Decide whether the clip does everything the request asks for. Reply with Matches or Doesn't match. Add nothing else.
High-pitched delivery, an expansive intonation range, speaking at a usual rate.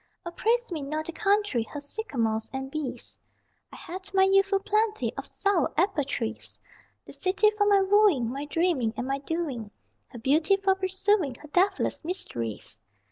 Matches